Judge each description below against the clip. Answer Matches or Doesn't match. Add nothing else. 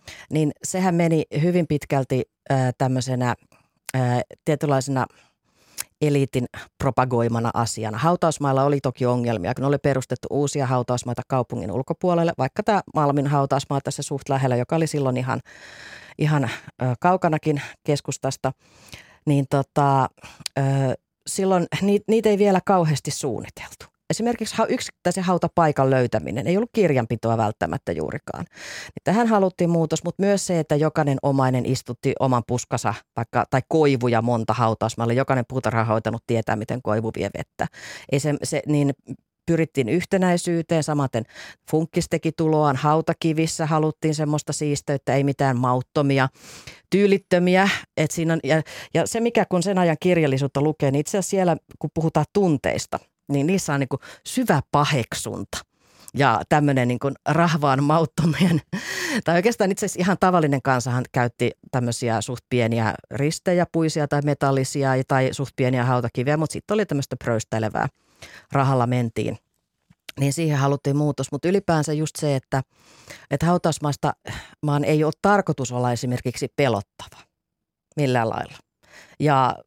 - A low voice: Doesn't match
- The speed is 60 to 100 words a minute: Doesn't match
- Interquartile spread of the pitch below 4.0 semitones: Doesn't match